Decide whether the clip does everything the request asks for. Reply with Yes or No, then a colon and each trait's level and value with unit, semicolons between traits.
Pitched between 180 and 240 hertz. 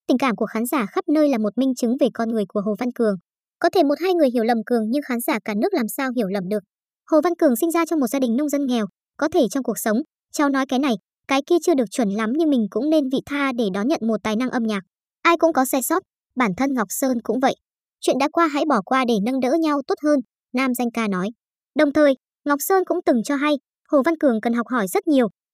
No: very high, 265 Hz